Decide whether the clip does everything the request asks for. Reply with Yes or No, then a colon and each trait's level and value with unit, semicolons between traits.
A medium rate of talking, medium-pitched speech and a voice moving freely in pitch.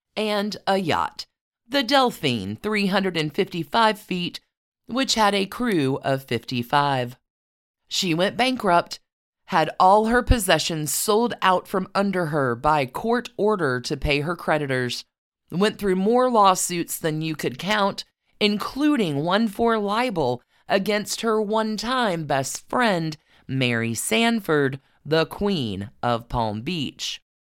No: slow, 125 wpm; medium, 180 Hz; wide, 7.3 semitones